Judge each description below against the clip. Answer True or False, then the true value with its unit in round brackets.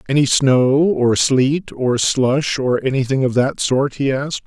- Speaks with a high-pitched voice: False (135 Hz)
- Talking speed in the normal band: True (175 wpm)